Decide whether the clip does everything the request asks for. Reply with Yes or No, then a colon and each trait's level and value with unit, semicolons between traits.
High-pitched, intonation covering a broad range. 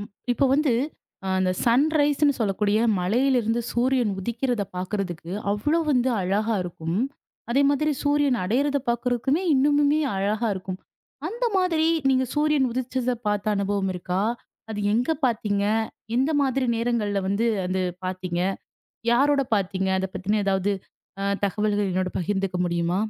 Yes: high, 225 Hz; wide, 5.7 semitones